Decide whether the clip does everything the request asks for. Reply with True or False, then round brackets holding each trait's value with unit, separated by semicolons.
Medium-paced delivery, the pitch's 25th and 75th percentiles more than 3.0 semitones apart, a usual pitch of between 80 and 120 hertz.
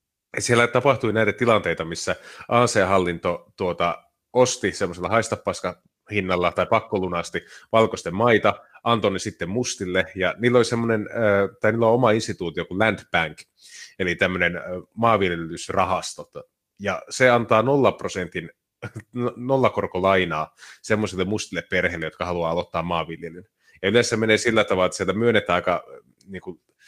True (120 wpm; 4.5 semitones; 105 Hz)